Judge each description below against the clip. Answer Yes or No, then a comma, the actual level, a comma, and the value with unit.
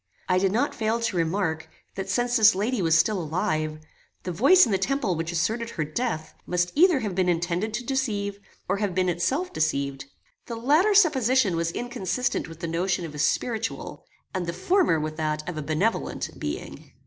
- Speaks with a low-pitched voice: No, high, 190 Hz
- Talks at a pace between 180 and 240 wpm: Yes, average, 190 wpm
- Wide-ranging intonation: Yes, wide, 6.1 semitones